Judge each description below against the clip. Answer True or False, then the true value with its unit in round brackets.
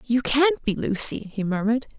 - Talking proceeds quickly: False (180 wpm)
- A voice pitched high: True (240 Hz)